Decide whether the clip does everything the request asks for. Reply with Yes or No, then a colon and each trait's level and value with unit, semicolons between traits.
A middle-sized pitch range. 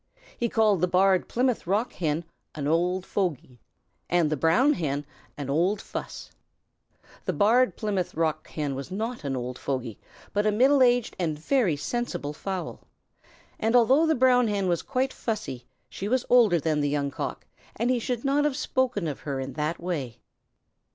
No: wide, 8.1 semitones